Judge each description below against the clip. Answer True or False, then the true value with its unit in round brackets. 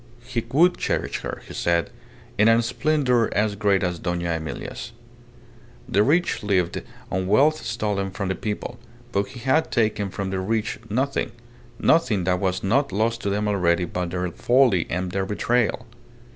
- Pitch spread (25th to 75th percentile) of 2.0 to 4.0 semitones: False (4.4 semitones)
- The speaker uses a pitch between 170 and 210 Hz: False (105 Hz)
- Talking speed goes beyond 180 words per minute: False (165 wpm)